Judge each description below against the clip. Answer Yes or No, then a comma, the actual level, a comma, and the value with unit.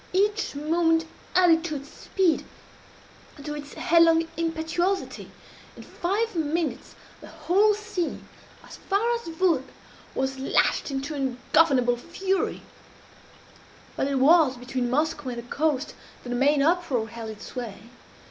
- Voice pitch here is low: No, very high, 310 Hz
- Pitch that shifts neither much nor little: Yes, average, 4.7 semitones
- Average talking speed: No, slow, 130 wpm